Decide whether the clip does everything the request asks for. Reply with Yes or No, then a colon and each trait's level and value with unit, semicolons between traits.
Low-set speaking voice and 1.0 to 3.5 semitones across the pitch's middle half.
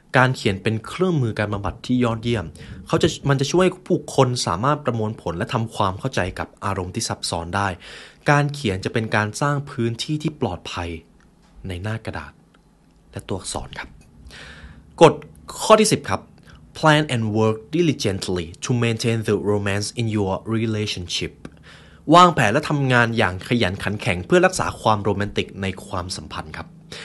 No: low, 110 Hz; average, 5.1 semitones